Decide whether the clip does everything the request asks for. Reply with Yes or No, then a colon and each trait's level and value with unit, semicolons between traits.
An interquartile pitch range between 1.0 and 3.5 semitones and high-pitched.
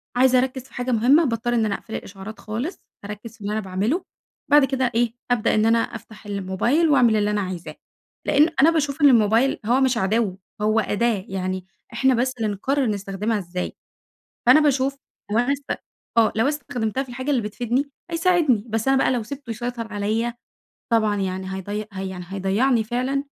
No: average, 4.1 semitones; high, 230 Hz